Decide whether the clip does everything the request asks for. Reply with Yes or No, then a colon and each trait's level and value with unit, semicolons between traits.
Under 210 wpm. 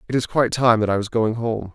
No: fast, 310 wpm